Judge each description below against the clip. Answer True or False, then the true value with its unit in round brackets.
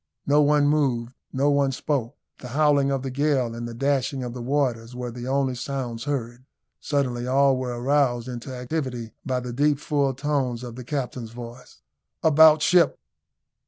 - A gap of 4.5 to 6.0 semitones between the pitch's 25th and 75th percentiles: False (2.7 semitones)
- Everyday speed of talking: True (170 wpm)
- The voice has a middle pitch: False (130 Hz)